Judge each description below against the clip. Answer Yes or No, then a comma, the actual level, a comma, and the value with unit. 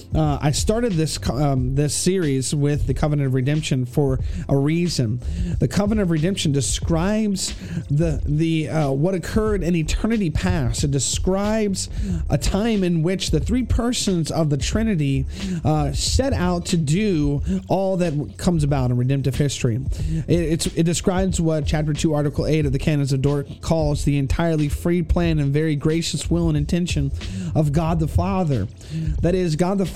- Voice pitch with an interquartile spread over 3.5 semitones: Yes, average, 4.1 semitones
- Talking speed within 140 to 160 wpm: No, average, 170 wpm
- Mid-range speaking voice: Yes, medium, 155 Hz